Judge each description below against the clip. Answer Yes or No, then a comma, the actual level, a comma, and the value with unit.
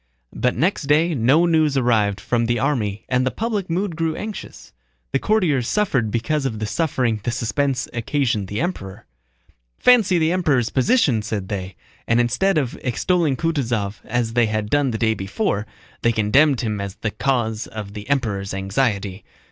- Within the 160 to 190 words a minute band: Yes, average, 170 wpm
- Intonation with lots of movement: Yes, wide, 6.2 semitones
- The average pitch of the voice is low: Yes, low, 125 Hz